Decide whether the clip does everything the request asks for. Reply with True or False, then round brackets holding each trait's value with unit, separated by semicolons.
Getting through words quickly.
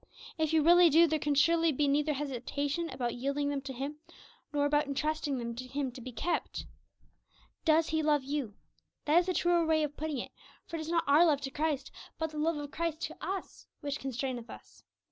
True (215 wpm)